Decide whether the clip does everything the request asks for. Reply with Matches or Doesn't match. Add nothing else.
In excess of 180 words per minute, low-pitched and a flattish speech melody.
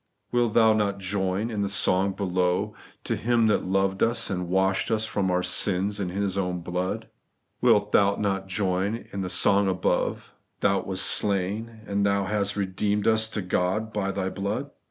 Matches